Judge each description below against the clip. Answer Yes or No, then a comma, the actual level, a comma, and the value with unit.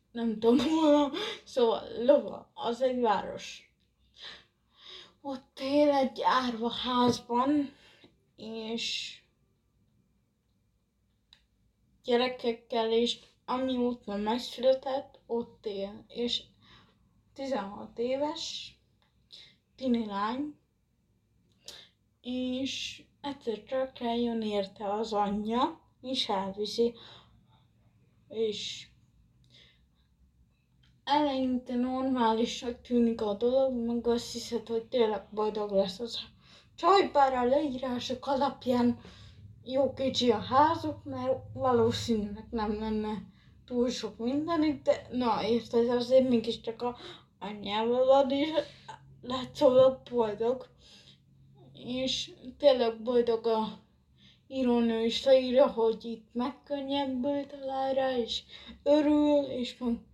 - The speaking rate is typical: No, slow, 90 wpm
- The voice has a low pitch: No, high, 245 Hz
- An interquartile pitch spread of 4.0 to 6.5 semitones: No, average, 2.8 semitones